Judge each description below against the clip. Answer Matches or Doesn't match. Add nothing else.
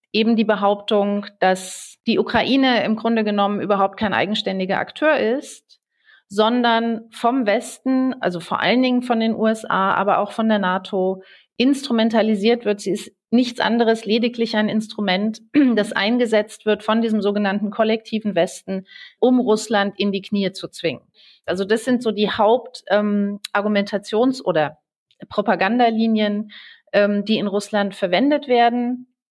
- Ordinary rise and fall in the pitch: Doesn't match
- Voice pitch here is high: Matches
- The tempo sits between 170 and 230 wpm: Doesn't match